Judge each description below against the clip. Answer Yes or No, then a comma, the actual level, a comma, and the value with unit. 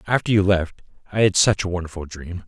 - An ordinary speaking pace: No, fast, 220 wpm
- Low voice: Yes, very low, 95 Hz